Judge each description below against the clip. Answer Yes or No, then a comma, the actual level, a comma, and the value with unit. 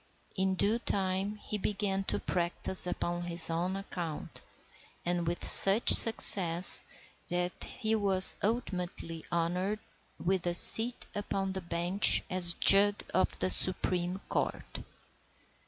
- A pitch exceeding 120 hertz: Yes, medium, 185 Hz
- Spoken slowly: Yes, slow, 120 wpm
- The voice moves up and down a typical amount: No, narrow, 2.3 semitones